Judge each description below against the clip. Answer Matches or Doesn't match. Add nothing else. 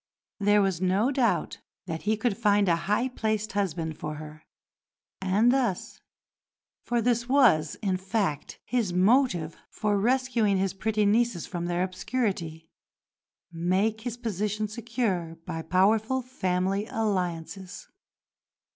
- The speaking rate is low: Matches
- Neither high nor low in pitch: Doesn't match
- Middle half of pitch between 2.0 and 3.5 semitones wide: Doesn't match